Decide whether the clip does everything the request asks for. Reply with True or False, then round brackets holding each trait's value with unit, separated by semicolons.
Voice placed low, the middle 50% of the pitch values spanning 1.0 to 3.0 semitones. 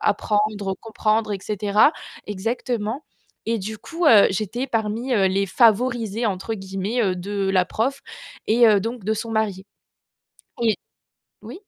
False (215 Hz; 2.7 semitones)